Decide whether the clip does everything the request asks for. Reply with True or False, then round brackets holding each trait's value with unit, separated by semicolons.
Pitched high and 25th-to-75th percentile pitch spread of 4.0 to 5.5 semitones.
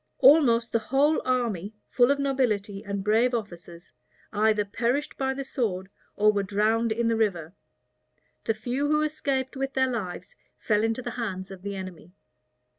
True (225 Hz; 4.6 semitones)